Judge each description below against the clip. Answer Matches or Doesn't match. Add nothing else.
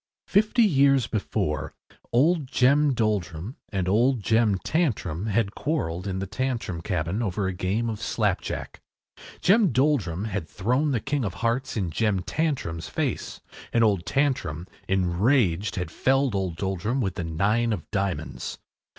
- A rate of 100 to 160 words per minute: Matches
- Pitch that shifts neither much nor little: Doesn't match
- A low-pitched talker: Matches